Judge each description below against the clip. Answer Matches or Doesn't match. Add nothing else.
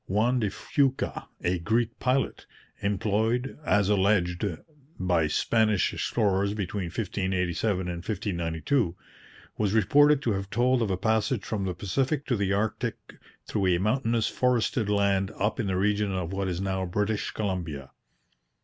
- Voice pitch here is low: Matches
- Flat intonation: Doesn't match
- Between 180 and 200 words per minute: Doesn't match